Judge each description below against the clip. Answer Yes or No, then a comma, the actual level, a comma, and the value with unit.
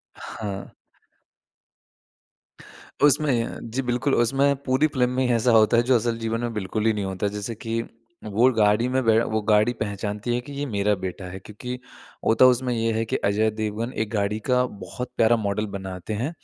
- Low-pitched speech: Yes, low, 115 Hz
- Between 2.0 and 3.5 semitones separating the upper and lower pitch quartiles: Yes, average, 2.9 semitones